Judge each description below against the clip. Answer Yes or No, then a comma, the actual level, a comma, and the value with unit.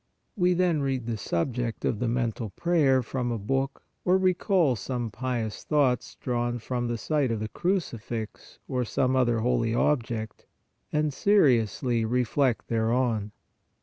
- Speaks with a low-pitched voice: Yes, low, 125 Hz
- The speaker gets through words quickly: No, average, 150 wpm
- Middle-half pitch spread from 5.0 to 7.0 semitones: No, average, 3.3 semitones